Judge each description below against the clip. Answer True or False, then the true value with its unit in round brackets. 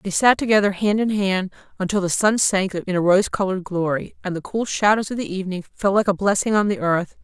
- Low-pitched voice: False (195 Hz)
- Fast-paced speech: True (240 wpm)